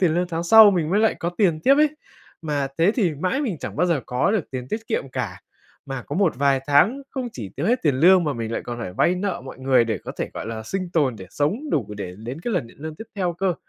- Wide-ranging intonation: Yes, wide, 6.8 semitones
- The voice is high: No, medium, 160 Hz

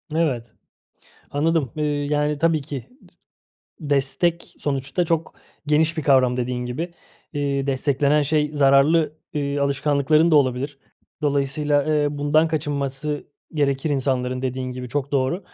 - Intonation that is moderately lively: No, narrow, 2.1 semitones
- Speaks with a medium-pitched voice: Yes, medium, 145 Hz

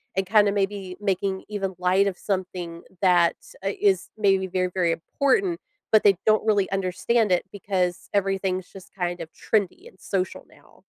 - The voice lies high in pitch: Yes, high, 195 Hz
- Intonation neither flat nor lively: No, narrow, 1.8 semitones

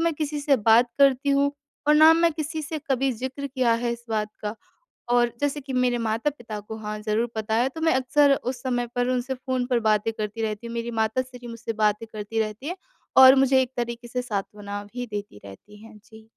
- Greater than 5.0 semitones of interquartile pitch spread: No, average, 3.3 semitones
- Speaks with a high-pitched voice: Yes, high, 240 Hz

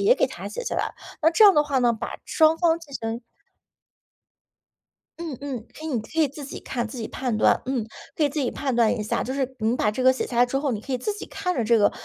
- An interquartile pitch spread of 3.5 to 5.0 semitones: Yes, average, 4.7 semitones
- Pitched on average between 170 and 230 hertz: No, very high, 265 Hz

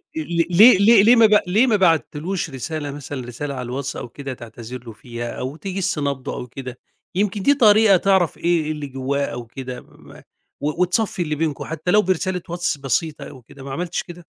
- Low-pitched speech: No, medium, 155 Hz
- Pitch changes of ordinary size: No, wide, 5.8 semitones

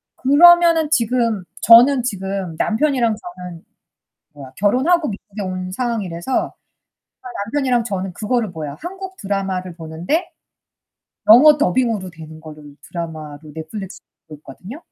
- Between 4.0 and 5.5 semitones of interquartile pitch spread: No, wide, 6.6 semitones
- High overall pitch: Yes, high, 205 Hz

